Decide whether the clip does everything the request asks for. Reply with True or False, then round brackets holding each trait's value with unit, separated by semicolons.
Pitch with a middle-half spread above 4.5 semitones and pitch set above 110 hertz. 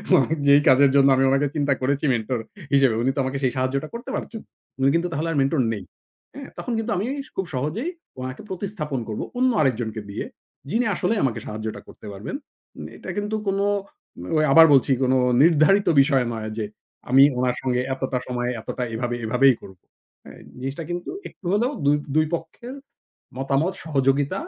True (4.9 semitones; 140 Hz)